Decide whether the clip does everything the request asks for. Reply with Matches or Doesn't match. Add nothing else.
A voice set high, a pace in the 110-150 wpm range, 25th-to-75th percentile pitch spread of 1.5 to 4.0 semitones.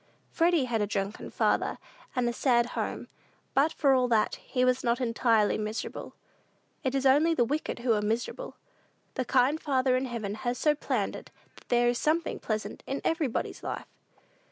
Doesn't match